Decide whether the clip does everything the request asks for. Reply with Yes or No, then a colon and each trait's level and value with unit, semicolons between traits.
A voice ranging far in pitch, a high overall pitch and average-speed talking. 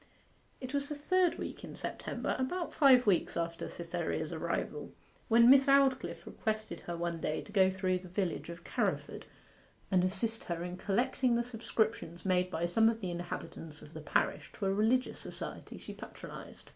Yes: wide, 6.3 semitones; high, 195 Hz; average, 175 wpm